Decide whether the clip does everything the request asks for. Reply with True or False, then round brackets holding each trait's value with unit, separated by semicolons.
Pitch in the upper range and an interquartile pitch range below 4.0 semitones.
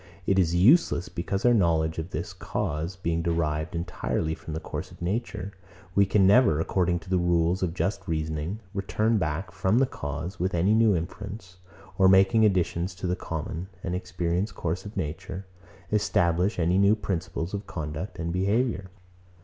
False (90 Hz; 2.9 semitones)